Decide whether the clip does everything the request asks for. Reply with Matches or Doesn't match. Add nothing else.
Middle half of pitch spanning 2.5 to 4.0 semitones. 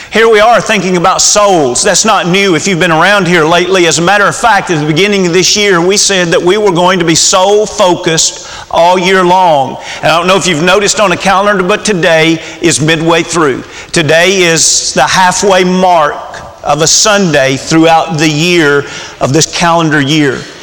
Matches